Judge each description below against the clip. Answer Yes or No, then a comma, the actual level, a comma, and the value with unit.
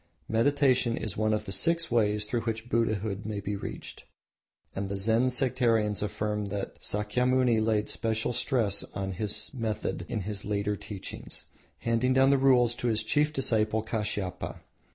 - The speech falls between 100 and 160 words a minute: Yes, average, 155 wpm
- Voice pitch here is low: Yes, low, 110 Hz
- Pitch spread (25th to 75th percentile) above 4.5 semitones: No, average, 2.8 semitones